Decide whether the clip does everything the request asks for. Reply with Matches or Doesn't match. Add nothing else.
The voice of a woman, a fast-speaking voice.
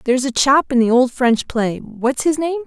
Matches